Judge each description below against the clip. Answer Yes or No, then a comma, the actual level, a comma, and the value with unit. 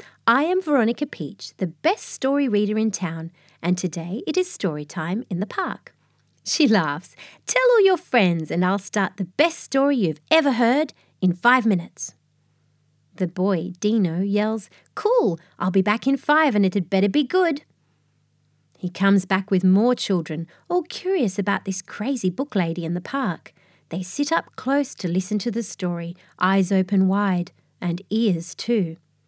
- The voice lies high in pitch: Yes, high, 195 Hz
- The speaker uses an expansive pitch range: Yes, wide, 6.5 semitones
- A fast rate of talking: No, average, 170 wpm